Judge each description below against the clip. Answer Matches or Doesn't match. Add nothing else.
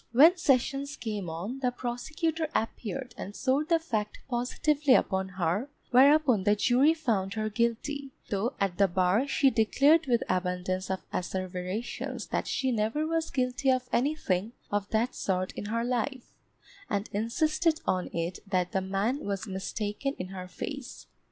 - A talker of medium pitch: Doesn't match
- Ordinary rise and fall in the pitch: Doesn't match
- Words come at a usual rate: Matches